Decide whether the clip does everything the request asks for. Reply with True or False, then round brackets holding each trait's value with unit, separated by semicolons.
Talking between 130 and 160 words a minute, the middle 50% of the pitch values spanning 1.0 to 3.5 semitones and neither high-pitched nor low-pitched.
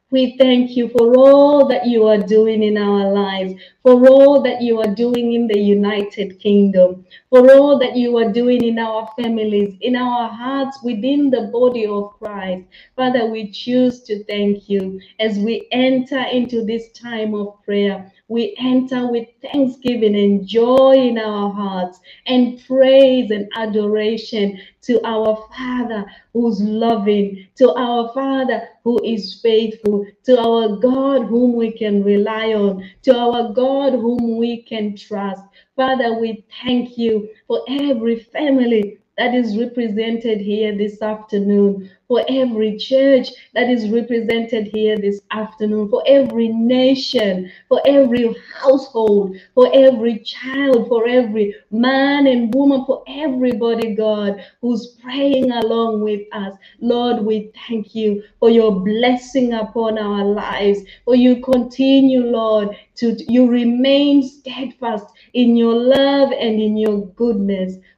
False (140 wpm; 3.0 semitones; 230 Hz)